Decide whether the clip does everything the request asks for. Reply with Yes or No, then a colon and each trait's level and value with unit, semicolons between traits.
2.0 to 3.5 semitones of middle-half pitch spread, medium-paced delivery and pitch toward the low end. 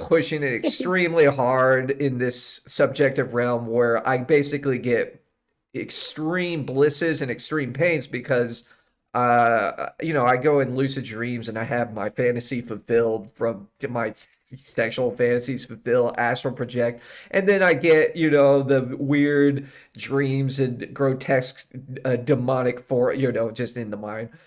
Yes: average, 2.8 semitones; average, 145 wpm; low, 130 Hz